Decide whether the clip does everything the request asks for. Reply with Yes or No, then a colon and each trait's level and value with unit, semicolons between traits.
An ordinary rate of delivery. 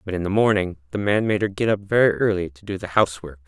No: fast, 275 wpm